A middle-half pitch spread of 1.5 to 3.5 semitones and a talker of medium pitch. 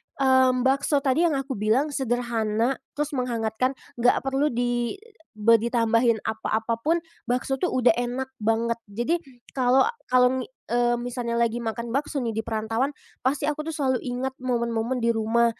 No: narrow, 2.4 semitones; high, 245 Hz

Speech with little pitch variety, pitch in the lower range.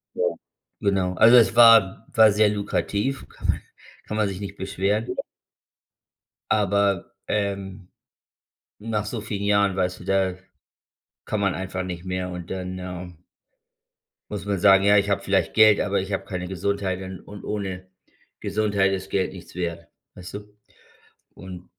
Yes: narrow, 1.9 semitones; very low, 95 Hz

